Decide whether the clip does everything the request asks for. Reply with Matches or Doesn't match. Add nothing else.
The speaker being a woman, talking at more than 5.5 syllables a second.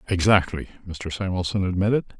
Doesn't match